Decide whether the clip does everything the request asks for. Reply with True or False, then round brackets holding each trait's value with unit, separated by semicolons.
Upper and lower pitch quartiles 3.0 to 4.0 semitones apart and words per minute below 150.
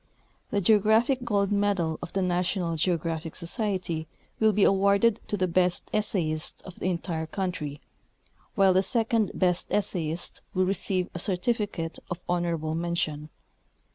True (3.3 semitones; 140 wpm)